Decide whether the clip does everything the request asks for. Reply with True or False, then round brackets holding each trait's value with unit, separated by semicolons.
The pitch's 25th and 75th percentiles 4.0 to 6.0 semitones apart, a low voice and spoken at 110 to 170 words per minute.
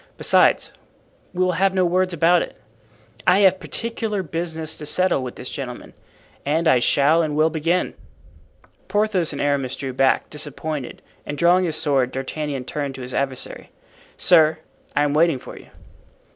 False (4.3 semitones; 155 Hz; 160 wpm)